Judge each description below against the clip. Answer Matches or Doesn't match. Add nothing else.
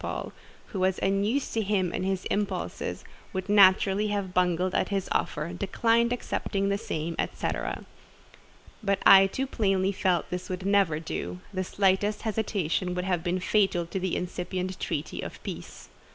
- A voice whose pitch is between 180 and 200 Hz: Matches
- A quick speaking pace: Doesn't match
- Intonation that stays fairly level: Matches